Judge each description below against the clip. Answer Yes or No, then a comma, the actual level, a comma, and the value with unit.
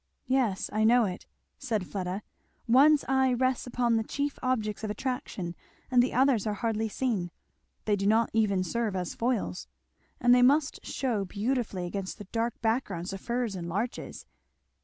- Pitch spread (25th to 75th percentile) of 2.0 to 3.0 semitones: No, average, 4.0 semitones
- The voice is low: No, high, 225 Hz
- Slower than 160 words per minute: No, average, 165 wpm